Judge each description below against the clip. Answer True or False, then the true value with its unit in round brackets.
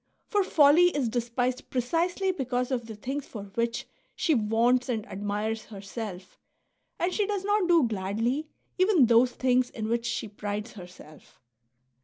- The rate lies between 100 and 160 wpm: True (150 wpm)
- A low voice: False (245 Hz)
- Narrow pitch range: False (5.4 semitones)